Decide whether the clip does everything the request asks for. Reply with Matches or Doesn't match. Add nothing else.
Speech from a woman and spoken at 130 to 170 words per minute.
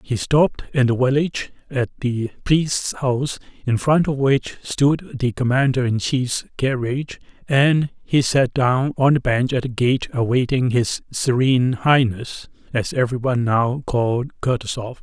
Doesn't match